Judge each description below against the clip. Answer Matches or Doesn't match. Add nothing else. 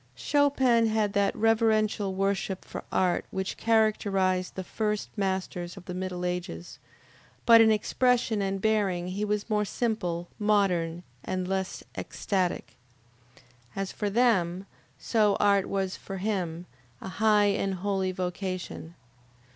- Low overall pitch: Doesn't match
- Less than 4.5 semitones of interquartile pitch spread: Matches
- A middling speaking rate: Doesn't match